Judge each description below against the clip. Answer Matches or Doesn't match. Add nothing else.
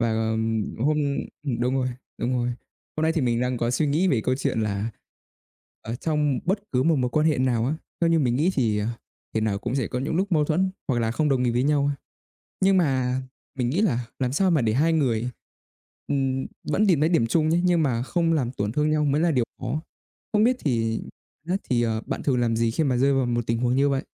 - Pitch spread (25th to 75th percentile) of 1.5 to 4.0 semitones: Doesn't match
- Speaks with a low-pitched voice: Matches